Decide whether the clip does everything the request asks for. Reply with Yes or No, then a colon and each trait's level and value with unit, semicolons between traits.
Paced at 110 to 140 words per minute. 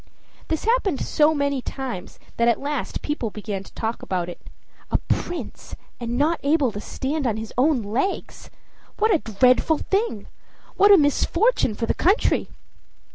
No: average, 160 wpm